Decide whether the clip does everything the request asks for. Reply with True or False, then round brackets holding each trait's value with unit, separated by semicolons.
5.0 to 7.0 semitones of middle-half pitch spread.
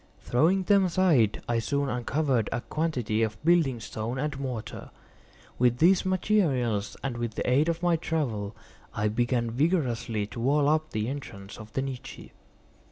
True (5.6 semitones)